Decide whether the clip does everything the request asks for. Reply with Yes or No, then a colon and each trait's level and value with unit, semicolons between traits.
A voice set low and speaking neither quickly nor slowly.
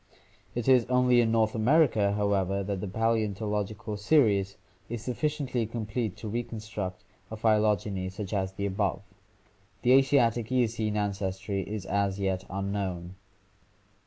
No: low, 105 Hz; slow, 130 wpm